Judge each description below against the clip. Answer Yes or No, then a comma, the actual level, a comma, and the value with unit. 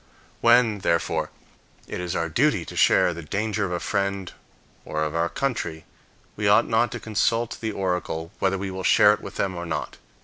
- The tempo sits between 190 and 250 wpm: Yes, average, 195 wpm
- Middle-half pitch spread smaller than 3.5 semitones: No, average, 4.2 semitones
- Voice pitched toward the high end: No, very low, 95 Hz